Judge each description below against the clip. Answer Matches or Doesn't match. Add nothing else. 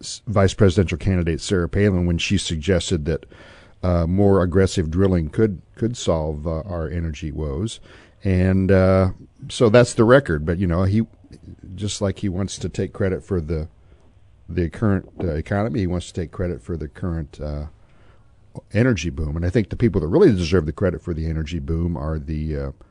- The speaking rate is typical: Matches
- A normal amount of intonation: Matches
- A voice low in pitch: Matches